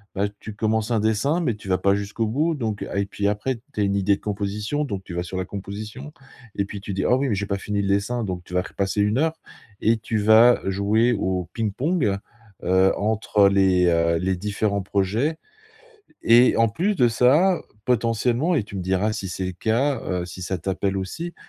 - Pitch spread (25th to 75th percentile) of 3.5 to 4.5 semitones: No, average, 3.1 semitones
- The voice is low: Yes, low, 105 Hz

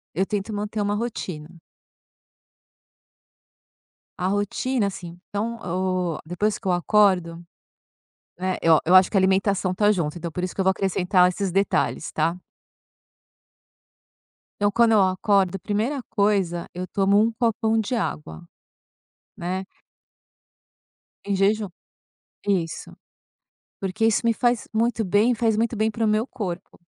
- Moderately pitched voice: No, high, 200 Hz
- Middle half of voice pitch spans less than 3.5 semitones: Yes, average, 3.1 semitones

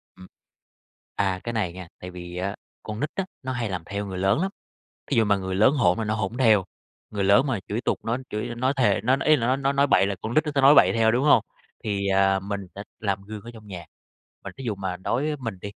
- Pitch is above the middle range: No, low, 105 Hz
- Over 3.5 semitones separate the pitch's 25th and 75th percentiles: Yes, average, 4.4 semitones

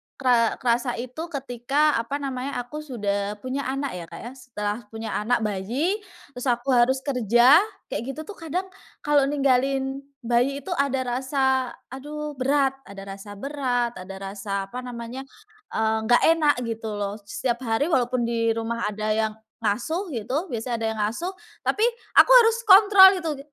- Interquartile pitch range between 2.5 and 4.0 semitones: Yes, average, 3.7 semitones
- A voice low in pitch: No, very high, 250 Hz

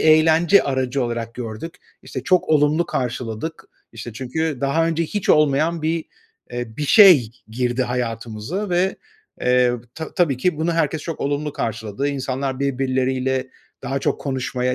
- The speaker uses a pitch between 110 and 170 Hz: Yes, low, 135 Hz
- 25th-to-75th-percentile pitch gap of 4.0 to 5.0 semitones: Yes, average, 4.4 semitones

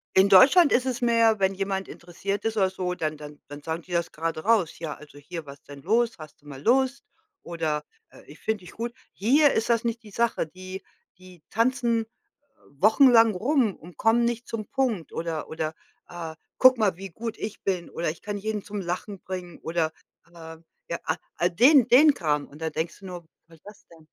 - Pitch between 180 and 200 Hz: Yes, high, 190 Hz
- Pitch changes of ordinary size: No, wide, 5.7 semitones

